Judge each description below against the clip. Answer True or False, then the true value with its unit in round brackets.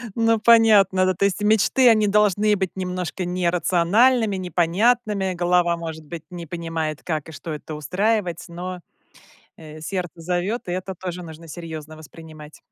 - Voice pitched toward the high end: False (180 Hz)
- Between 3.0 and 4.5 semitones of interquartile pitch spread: True (3.5 semitones)